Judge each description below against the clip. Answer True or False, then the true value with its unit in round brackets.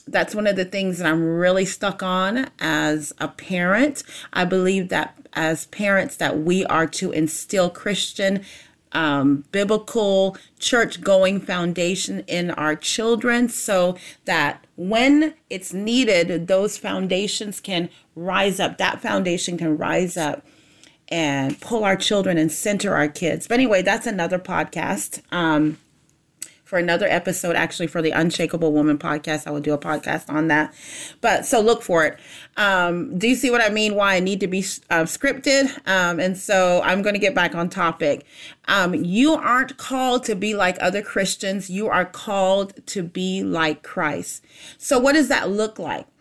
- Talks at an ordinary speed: True (165 wpm)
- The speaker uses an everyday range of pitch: True (3.6 semitones)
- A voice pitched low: False (185 Hz)